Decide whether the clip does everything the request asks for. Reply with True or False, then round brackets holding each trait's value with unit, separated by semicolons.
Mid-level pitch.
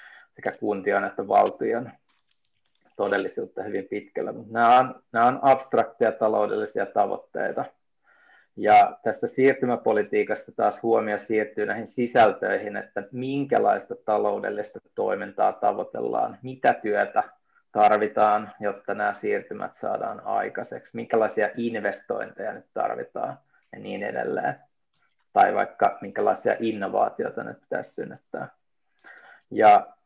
False (115 Hz)